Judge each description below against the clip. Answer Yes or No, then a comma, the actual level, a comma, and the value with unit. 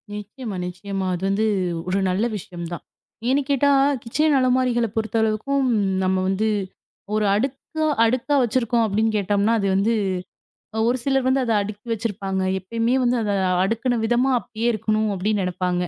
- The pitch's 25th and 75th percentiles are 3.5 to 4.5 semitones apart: Yes, average, 3.9 semitones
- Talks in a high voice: Yes, high, 220 Hz